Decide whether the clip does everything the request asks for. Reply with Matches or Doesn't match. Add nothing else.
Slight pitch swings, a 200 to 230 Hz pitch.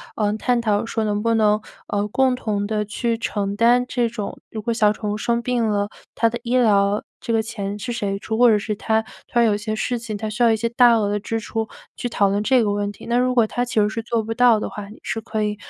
Matches